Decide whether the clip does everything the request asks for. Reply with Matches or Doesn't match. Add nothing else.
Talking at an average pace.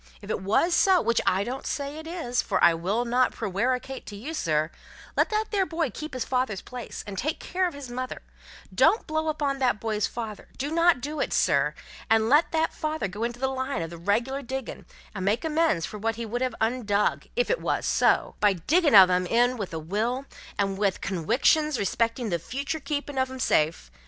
Doesn't match